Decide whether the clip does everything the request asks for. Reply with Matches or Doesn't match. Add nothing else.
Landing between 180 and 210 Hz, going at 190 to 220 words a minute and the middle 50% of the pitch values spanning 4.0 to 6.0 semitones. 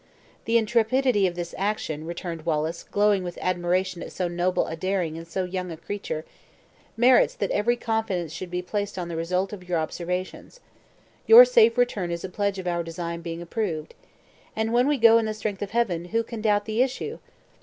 Matches